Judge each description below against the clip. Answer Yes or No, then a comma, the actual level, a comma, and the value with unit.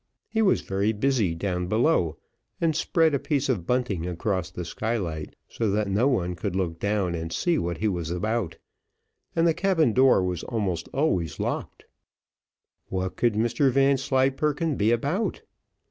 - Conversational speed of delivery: Yes, average, 160 wpm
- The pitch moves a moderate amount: No, wide, 7.1 semitones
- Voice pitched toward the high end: No, low, 110 Hz